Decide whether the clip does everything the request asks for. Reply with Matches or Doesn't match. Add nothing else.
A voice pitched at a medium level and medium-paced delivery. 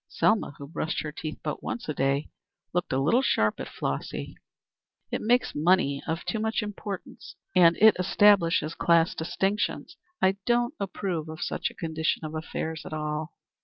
Matches